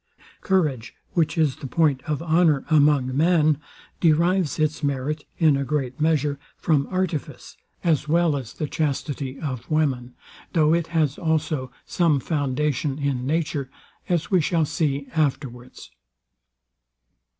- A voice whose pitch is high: No, medium, 150 Hz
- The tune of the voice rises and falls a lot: No, average, 2.8 semitones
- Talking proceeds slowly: Yes, slow, 130 wpm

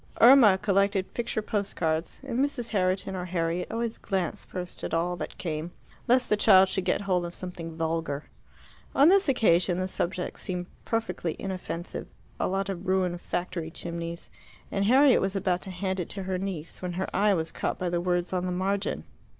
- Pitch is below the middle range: No, medium, 185 Hz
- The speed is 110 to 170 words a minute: No, average, 190 wpm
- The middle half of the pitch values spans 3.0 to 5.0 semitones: No, narrow, 2.5 semitones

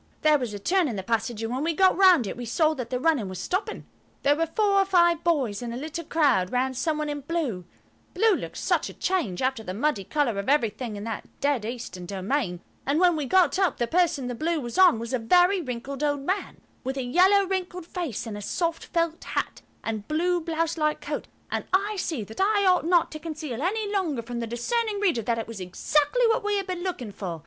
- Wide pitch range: Yes, wide, 7.2 semitones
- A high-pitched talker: Yes, very high, 295 Hz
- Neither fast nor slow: No, fast, 230 wpm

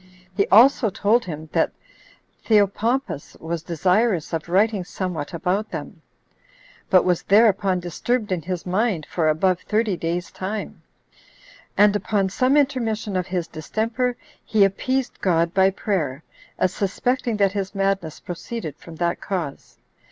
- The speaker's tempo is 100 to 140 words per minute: Yes, slow, 135 wpm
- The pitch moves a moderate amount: Yes, average, 3.9 semitones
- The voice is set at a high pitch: Yes, high, 195 Hz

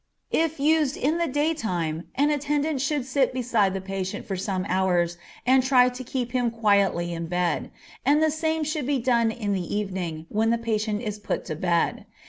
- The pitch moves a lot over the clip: Yes, wide, 6.8 semitones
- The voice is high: Yes, high, 230 Hz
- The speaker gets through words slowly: No, average, 190 wpm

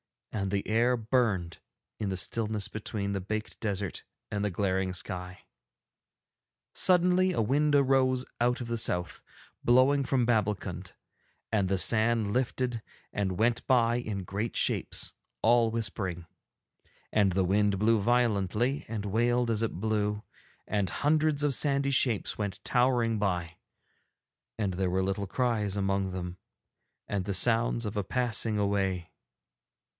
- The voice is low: Yes, low, 110 Hz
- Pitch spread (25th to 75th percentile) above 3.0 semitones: Yes, average, 3.8 semitones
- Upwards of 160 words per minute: No, average, 140 wpm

